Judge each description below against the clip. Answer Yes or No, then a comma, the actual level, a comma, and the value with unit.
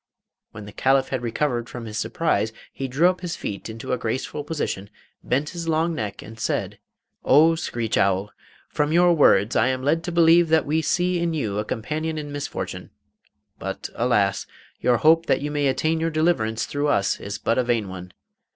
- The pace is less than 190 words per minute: No, average, 195 wpm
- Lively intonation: Yes, wide, 6.4 semitones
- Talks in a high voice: No, medium, 140 Hz